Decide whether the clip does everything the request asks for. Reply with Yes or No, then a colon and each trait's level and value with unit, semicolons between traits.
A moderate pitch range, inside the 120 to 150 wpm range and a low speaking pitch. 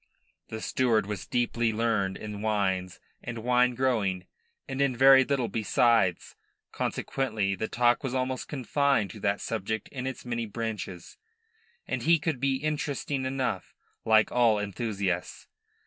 Yes: average, 3.9 semitones; average, 140 wpm; low, 115 Hz